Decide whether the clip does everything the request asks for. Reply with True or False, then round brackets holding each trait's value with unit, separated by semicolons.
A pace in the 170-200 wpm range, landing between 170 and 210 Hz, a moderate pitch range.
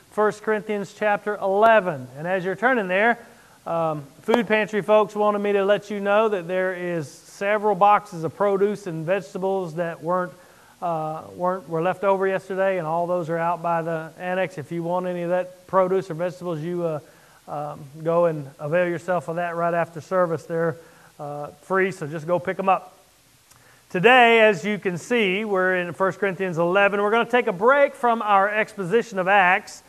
True (190 wpm; 185 Hz; 3.3 semitones)